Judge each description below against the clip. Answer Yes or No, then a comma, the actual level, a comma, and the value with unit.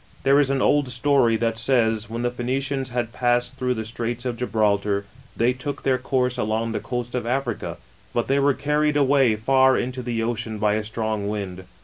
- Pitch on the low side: Yes, low, 120 Hz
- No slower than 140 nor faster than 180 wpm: No, average, 200 wpm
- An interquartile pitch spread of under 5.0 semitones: Yes, average, 2.9 semitones